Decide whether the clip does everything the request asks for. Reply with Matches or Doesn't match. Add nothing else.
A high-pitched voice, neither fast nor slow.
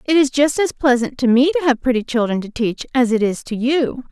Doesn't match